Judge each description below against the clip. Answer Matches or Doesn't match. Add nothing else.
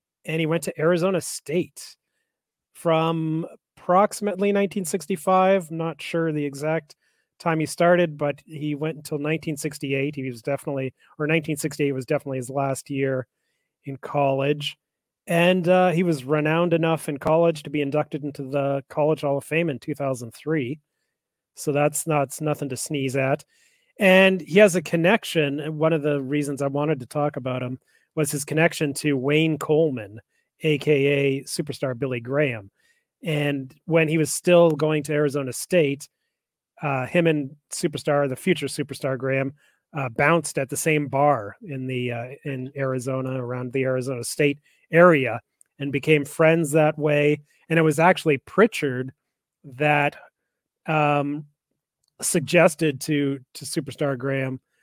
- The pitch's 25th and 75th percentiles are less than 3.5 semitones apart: Matches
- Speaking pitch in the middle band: Matches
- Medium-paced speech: Matches